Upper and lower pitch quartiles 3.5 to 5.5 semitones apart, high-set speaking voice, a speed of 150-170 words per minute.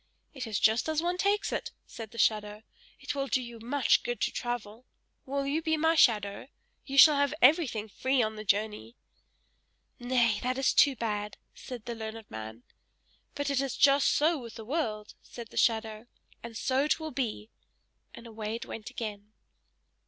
No: average, 4.4 semitones; high, 240 Hz; average, 180 wpm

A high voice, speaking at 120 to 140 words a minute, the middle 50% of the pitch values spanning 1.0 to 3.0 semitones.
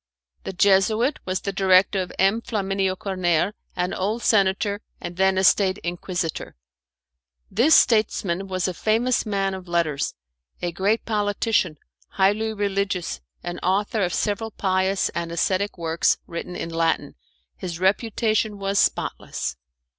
Yes: high, 195 Hz; slow, 135 wpm; narrow, 2.4 semitones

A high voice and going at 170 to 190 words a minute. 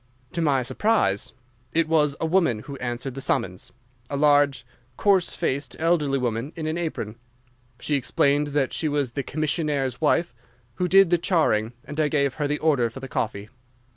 No: medium, 145 Hz; average, 175 wpm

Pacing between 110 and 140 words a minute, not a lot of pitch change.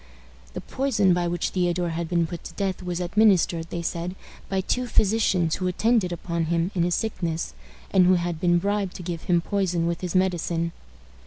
No: average, 190 wpm; narrow, 2.0 semitones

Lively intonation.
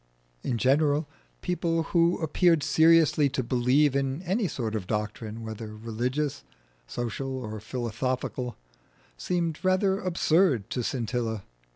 Yes: wide, 6.1 semitones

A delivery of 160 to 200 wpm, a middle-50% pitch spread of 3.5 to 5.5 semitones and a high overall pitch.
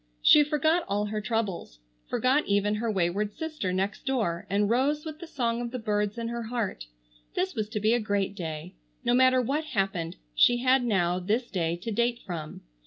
Yes: average, 195 wpm; average, 4.3 semitones; high, 215 Hz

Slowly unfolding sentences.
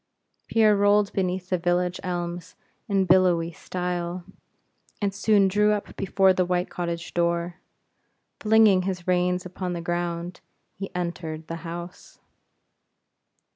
Yes: slow, 125 wpm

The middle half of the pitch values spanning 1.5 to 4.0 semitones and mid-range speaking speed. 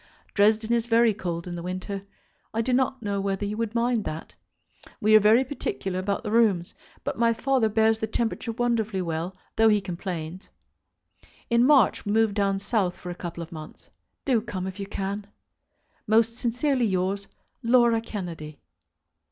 Yes: average, 3.6 semitones; average, 170 wpm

